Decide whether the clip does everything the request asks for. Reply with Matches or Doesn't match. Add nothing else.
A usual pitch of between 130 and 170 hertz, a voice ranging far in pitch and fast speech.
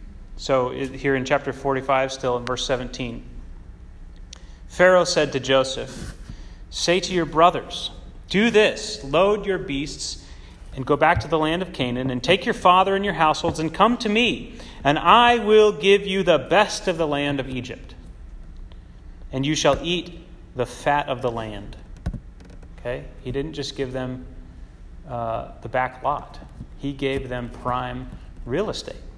Doesn't match